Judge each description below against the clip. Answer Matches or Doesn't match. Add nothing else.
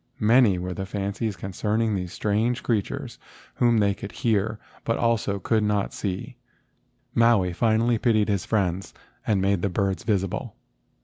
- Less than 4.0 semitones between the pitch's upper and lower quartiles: Matches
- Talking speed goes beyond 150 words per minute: Doesn't match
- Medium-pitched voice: Doesn't match